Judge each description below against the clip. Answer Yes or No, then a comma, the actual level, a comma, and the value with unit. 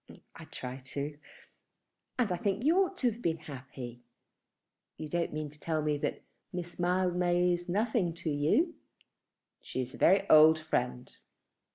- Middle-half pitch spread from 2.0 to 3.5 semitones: No, average, 4.2 semitones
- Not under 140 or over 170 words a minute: Yes, average, 160 wpm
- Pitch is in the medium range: Yes, medium, 170 Hz